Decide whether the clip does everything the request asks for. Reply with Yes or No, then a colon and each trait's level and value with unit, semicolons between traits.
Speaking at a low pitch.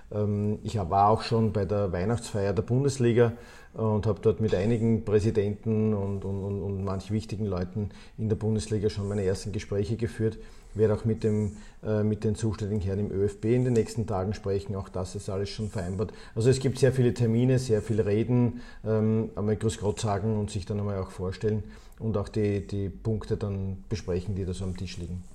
Yes: low, 105 Hz